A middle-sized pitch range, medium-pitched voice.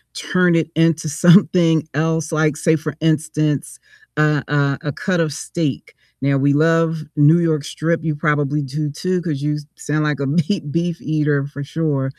No: narrow, 2.0 semitones; medium, 155 Hz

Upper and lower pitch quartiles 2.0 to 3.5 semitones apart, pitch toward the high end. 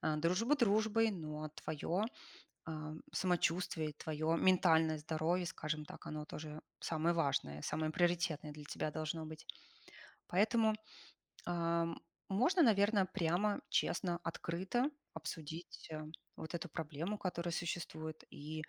No: average, 3.0 semitones; medium, 165 Hz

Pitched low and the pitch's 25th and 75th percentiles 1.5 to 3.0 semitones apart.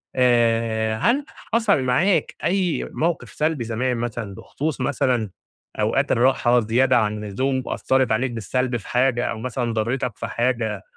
Yes: low, 125 Hz; average, 2.7 semitones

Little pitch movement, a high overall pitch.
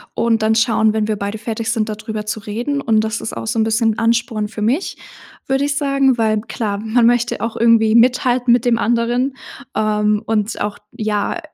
Yes: narrow, 1.9 semitones; high, 225 Hz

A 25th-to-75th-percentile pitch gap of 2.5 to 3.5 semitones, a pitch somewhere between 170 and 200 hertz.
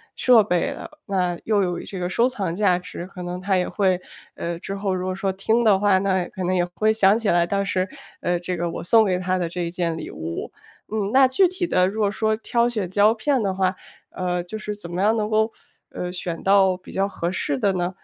Yes: average, 2.9 semitones; high, 190 Hz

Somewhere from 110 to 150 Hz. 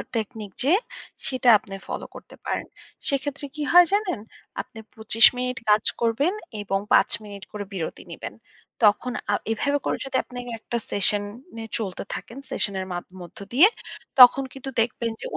No: high, 230 Hz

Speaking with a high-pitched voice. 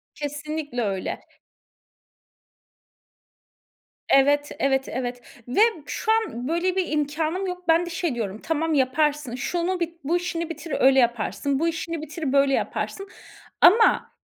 Yes: very high, 305 Hz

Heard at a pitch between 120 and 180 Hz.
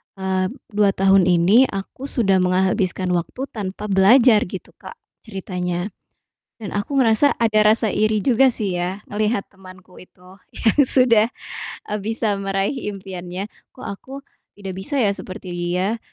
No: high, 195 Hz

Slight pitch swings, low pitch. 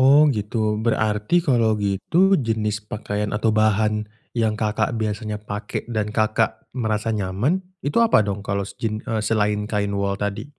Yes: narrow, 1.5 semitones; low, 110 Hz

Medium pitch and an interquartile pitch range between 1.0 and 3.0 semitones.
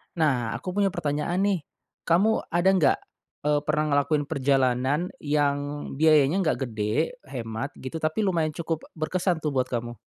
No: medium, 150 Hz; average, 3.8 semitones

